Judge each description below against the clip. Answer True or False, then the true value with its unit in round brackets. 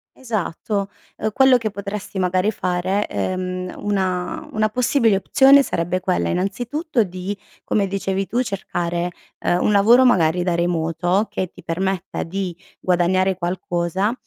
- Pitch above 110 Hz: True (190 Hz)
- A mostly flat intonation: False (3.1 semitones)